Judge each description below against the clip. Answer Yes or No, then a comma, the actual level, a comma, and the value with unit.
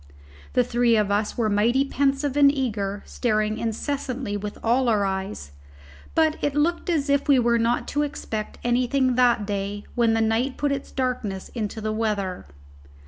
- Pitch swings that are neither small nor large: Yes, average, 4.3 semitones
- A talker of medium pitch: No, high, 235 Hz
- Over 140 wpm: Yes, average, 170 wpm